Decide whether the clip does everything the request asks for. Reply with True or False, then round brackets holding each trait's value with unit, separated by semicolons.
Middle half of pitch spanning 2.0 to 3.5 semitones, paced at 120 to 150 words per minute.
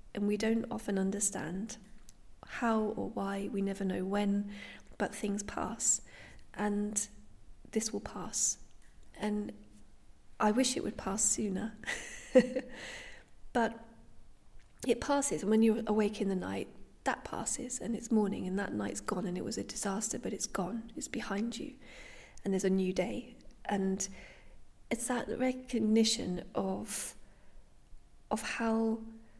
True (2.8 semitones; 140 wpm)